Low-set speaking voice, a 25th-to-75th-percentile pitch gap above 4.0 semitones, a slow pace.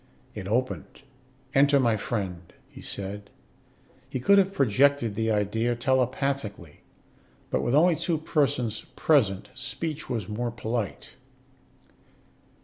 Yes: low, 120 Hz; average, 4.9 semitones; slow, 115 wpm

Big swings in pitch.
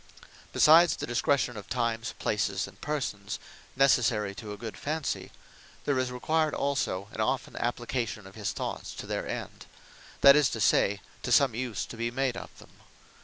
No: average, 4.5 semitones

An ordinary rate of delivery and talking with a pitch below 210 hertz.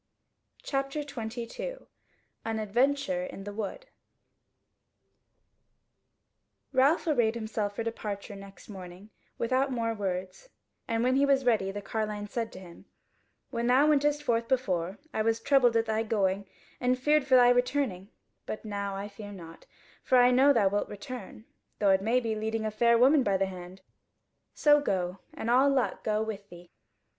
No: average, 165 wpm; high, 225 Hz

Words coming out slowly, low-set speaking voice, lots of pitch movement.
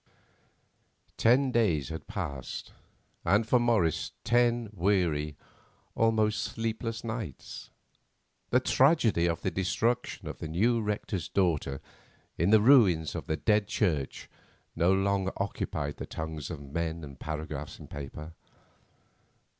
Yes: slow, 120 wpm; very low, 95 Hz; wide, 6.2 semitones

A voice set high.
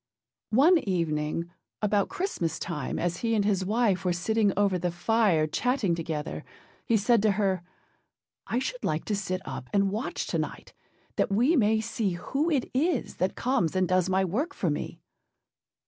Yes: high, 200 Hz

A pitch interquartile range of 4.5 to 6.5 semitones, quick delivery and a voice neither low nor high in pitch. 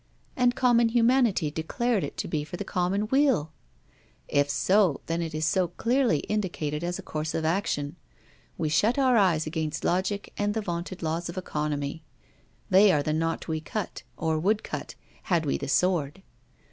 No: average, 5.2 semitones; average, 170 wpm; medium, 175 Hz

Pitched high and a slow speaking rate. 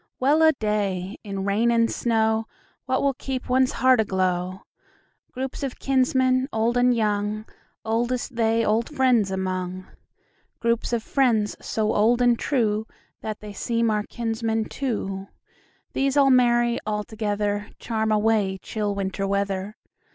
Yes: high, 220 Hz; slow, 120 wpm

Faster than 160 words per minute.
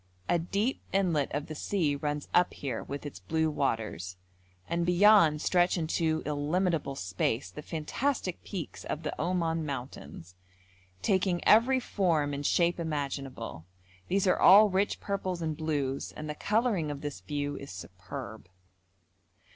No: average, 145 wpm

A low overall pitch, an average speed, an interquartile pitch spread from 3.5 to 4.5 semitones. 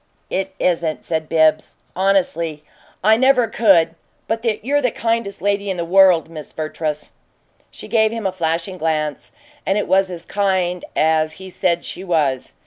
No: medium, 180 Hz; average, 160 wpm; average, 3.8 semitones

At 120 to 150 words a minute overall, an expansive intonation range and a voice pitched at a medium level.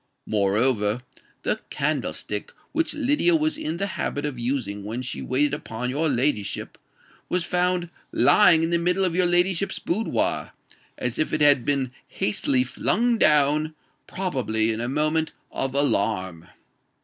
Yes: average, 140 wpm; wide, 6.5 semitones; medium, 145 Hz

